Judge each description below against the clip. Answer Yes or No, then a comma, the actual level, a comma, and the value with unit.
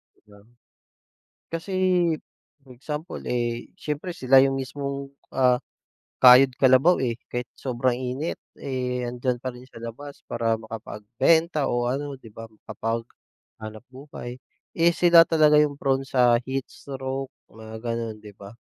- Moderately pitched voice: No, low, 130 Hz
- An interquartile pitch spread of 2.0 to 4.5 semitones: Yes, average, 2.8 semitones